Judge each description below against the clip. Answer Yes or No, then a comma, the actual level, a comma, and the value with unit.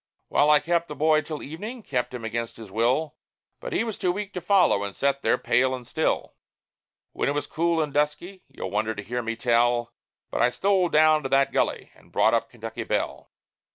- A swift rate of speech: Yes, fast, 215 wpm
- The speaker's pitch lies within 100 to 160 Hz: Yes, medium, 140 Hz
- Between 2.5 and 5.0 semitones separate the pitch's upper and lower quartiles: No, wide, 5.6 semitones